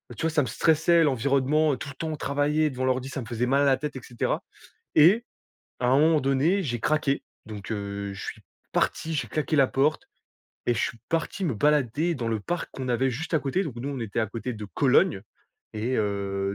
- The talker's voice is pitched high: No, low, 135 Hz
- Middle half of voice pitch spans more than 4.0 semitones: Yes, average, 4.7 semitones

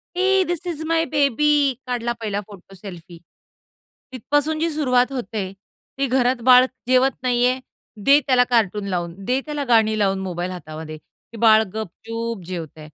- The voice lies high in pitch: Yes, high, 240 Hz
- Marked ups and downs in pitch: Yes, wide, 5.9 semitones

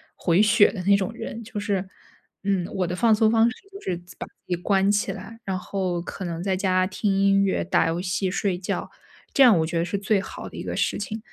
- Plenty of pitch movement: No, narrow, 2.4 semitones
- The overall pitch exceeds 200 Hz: No, high, 195 Hz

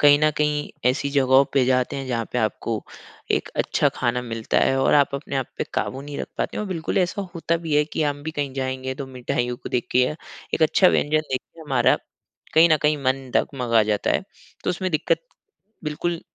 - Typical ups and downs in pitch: Yes, average, 3.1 semitones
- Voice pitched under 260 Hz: Yes, medium, 140 Hz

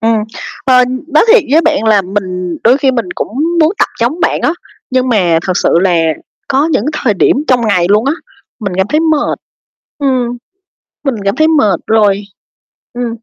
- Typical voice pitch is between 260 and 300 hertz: No, high, 240 Hz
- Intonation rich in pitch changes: Yes, wide, 6.0 semitones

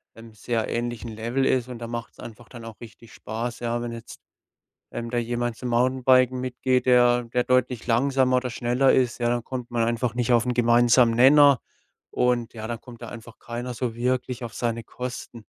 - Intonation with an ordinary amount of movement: No, narrow, 1.3 semitones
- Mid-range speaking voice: No, low, 120 Hz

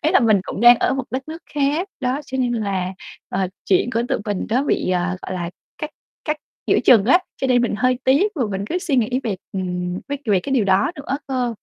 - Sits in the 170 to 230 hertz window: No, high, 245 Hz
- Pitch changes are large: Yes, wide, 5.9 semitones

